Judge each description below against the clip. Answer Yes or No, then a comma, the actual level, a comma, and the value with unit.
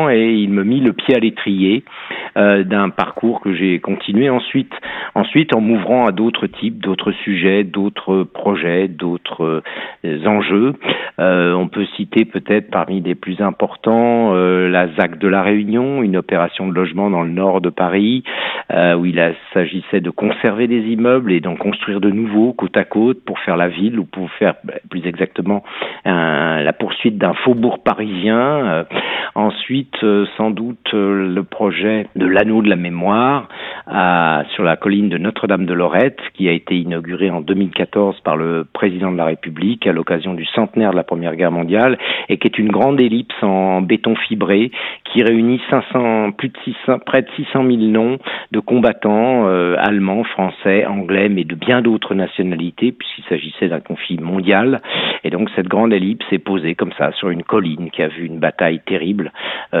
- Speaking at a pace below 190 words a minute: Yes, average, 180 wpm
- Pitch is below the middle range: Yes, low, 100 Hz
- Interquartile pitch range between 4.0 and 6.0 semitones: No, average, 3.6 semitones